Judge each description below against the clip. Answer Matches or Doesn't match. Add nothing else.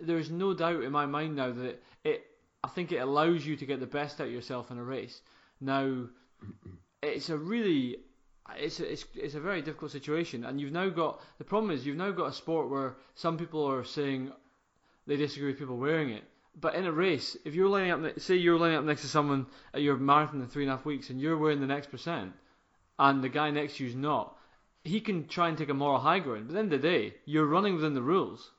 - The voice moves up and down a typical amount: Matches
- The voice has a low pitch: Doesn't match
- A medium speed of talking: Doesn't match